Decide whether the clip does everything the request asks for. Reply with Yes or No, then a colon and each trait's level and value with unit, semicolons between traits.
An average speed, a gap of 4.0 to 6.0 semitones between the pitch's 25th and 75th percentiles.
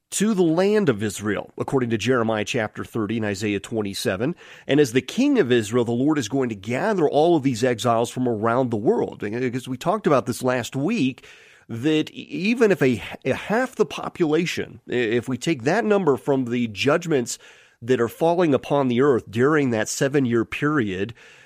Yes: average, 185 wpm; average, 4.7 semitones